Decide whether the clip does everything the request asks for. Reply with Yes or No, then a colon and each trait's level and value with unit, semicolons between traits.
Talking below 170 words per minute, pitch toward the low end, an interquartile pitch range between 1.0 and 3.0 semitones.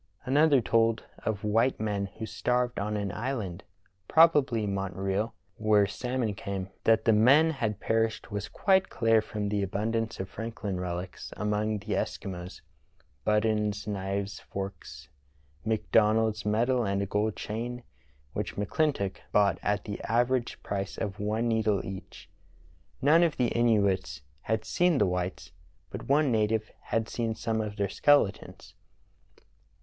Yes: average, 145 wpm; low, 110 Hz; narrow, 2.6 semitones